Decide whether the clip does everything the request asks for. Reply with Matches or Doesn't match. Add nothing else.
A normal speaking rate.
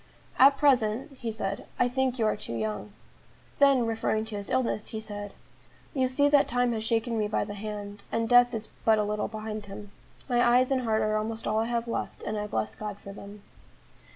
Doesn't match